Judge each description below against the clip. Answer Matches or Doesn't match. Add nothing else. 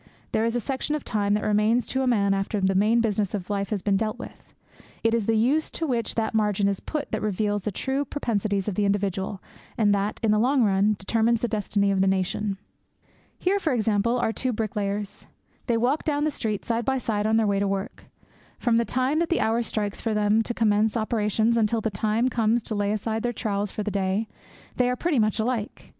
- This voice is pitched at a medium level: Doesn't match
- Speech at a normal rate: Doesn't match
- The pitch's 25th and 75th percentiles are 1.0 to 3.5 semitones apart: Matches